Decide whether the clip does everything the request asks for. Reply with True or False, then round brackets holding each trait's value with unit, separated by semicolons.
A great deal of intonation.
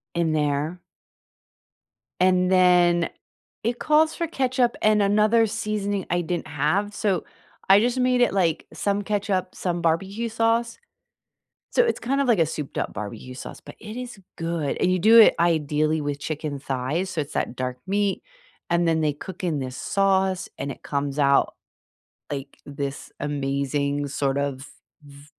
True (6.2 semitones)